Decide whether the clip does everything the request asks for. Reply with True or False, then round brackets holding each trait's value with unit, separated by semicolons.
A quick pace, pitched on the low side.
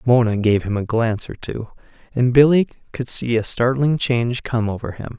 False (195 wpm; 120 Hz)